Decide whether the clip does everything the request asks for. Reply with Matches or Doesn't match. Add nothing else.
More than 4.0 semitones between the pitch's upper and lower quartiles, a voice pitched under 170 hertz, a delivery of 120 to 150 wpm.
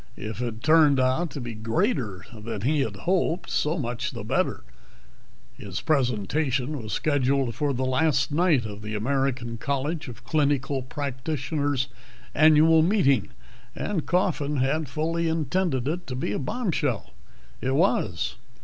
Matches